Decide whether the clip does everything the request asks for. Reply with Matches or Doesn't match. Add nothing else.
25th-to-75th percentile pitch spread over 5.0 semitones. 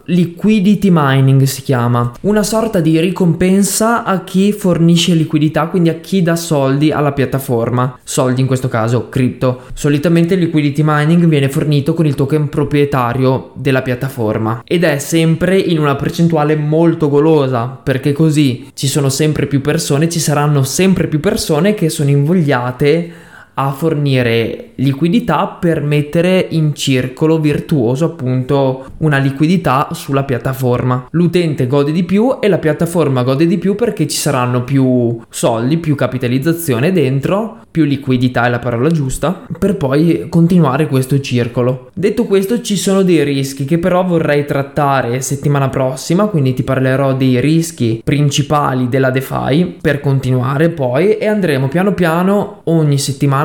Doesn't match